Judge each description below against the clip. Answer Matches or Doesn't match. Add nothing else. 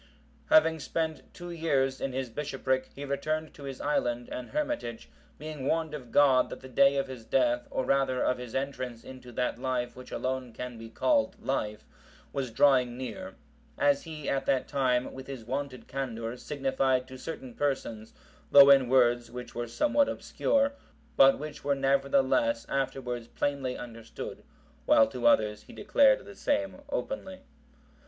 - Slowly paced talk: Doesn't match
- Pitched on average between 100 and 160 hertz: Matches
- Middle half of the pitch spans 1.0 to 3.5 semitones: Matches